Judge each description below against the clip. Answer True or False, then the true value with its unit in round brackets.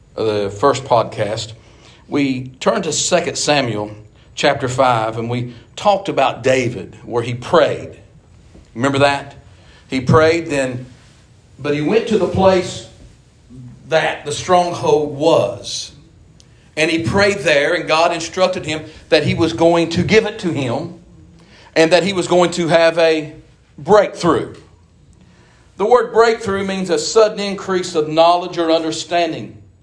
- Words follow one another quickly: False (140 wpm)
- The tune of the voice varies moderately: False (6.2 semitones)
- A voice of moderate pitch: True (155 Hz)